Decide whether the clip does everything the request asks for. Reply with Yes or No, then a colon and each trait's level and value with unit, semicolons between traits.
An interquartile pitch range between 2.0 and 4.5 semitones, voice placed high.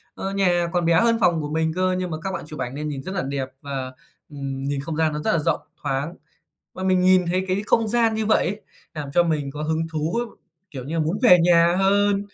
No: average, 3.8 semitones; medium, 170 Hz